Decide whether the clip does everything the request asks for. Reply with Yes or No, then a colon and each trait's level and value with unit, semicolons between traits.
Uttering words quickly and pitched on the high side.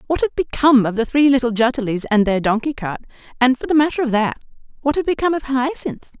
Yes: fast, 225 wpm; very high, 255 Hz